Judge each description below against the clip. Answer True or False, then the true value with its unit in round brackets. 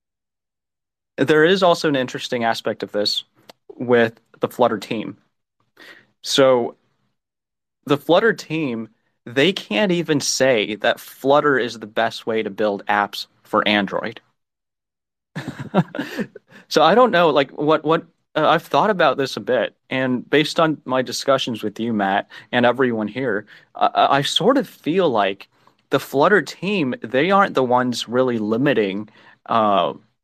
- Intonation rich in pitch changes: False (5.0 semitones)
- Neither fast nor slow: True (145 wpm)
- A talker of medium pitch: False (125 Hz)